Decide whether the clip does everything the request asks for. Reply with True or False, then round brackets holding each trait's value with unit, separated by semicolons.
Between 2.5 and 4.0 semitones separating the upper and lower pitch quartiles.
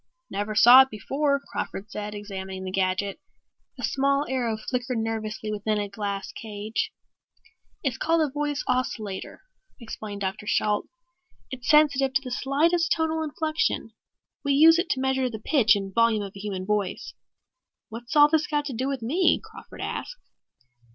False (5.4 semitones)